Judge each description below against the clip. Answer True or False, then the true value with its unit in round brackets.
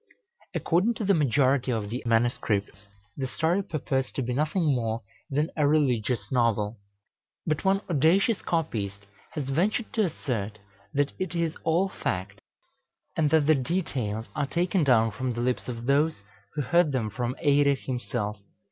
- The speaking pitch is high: False (135 Hz)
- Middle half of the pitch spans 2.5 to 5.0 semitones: False (5.6 semitones)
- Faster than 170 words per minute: False (155 wpm)